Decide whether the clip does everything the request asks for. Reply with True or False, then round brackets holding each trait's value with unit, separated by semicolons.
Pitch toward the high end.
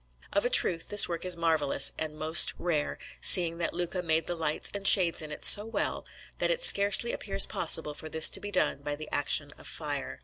False (165 Hz)